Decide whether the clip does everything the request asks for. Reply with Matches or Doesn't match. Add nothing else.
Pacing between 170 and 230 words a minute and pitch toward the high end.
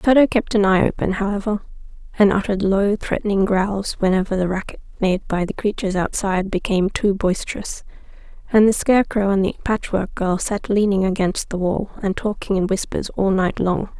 Matches